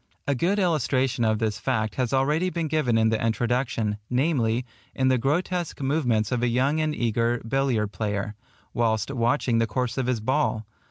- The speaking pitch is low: Yes, low, 125 Hz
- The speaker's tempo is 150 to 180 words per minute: Yes, average, 175 wpm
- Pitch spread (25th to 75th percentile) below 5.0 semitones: Yes, average, 3.8 semitones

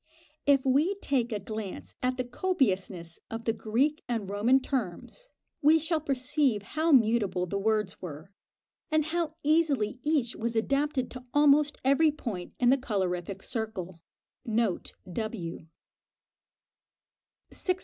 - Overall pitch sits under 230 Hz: No, high, 245 Hz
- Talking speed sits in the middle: No, slow, 130 wpm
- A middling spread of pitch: No, wide, 6.1 semitones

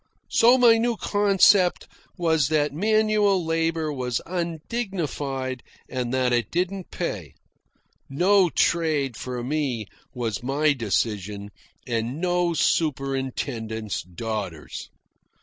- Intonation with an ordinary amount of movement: No, wide, 6.5 semitones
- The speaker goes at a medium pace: No, slow, 100 wpm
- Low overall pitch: No, medium, 150 Hz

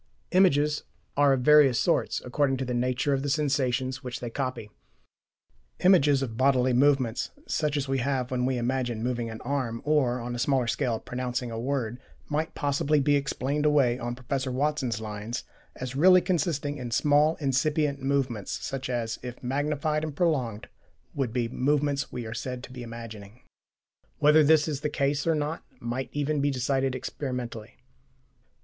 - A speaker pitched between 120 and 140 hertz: Yes, low, 135 Hz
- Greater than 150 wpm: Yes, average, 170 wpm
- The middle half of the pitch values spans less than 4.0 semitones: Yes, average, 2.9 semitones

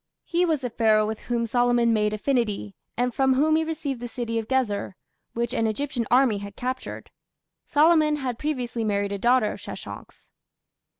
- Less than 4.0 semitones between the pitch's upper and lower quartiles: Yes, average, 3.6 semitones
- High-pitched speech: Yes, high, 245 Hz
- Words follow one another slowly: No, average, 175 wpm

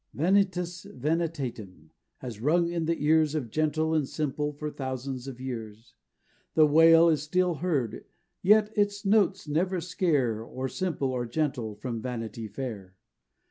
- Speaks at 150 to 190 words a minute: No, average, 140 wpm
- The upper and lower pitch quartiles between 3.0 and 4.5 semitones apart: No, average, 5.3 semitones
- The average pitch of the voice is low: No, medium, 150 Hz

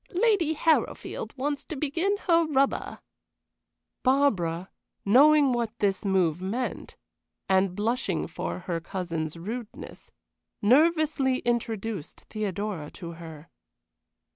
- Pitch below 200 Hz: No, high, 225 Hz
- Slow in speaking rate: Yes, slow, 100 wpm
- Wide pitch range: Yes, wide, 7.5 semitones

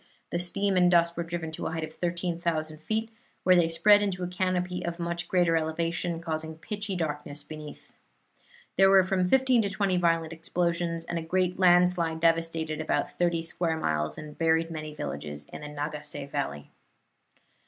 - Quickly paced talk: No, average, 175 wpm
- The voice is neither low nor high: Yes, medium, 170 Hz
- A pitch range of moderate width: No, narrow, 2.2 semitones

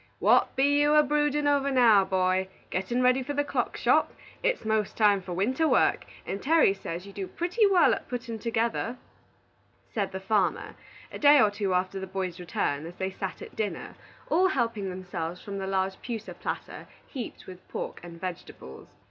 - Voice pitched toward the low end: No, high, 205 Hz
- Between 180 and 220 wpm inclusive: Yes, average, 185 wpm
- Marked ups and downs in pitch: Yes, wide, 6.0 semitones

